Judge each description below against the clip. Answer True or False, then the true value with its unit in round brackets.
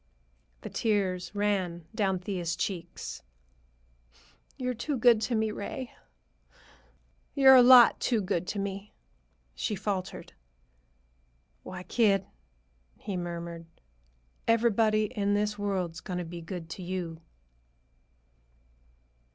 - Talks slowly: True (110 wpm)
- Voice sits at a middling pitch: False (200 Hz)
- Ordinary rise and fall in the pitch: True (3.4 semitones)